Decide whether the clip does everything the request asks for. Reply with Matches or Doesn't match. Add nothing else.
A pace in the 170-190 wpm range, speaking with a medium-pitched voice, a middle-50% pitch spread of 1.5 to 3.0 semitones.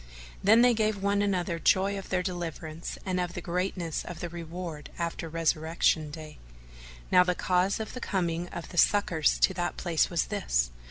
Matches